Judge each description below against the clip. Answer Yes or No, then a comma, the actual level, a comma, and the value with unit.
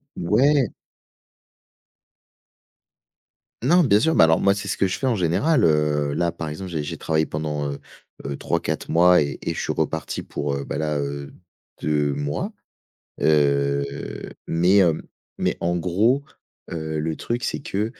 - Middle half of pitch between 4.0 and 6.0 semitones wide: Yes, average, 4.9 semitones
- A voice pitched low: Yes, very low, 80 Hz